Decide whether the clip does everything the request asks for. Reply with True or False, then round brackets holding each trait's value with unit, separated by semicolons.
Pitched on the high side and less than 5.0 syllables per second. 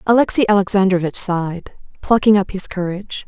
False (195 Hz; 5.8 syllables/s)